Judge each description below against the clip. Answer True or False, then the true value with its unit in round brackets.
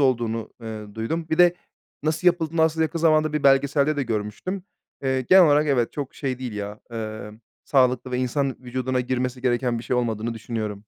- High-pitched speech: False (130 Hz)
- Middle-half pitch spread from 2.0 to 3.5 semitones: False (4.9 semitones)